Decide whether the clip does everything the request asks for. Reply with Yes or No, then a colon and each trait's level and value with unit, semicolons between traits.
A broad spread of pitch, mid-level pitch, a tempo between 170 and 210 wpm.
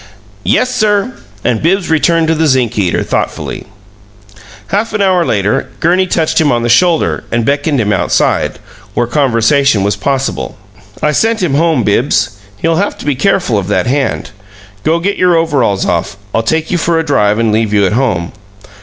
Yes: wide, 6.8 semitones; medium, 145 Hz; average, 180 wpm